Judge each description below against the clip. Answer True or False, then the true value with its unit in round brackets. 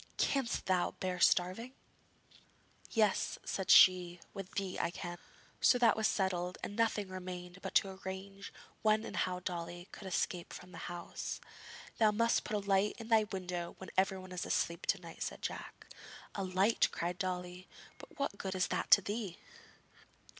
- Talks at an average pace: True (170 wpm)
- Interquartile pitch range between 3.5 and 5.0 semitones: False (2.5 semitones)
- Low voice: False (190 Hz)